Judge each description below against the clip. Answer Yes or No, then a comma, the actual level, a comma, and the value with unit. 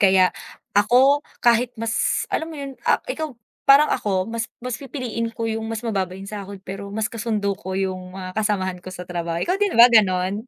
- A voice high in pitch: Yes, high, 215 Hz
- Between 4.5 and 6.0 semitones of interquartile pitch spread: No, average, 4.0 semitones